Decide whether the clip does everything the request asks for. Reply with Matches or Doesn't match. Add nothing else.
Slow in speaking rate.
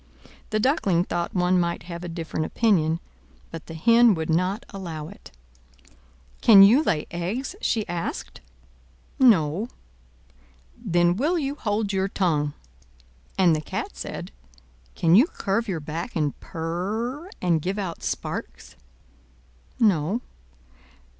Matches